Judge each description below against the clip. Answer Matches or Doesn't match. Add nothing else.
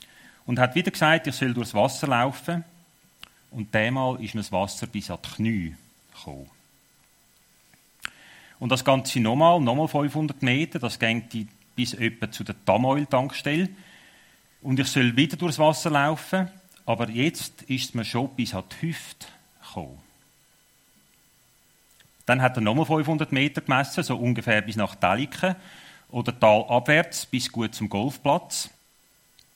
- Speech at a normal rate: Matches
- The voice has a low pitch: Matches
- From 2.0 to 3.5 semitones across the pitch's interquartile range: Doesn't match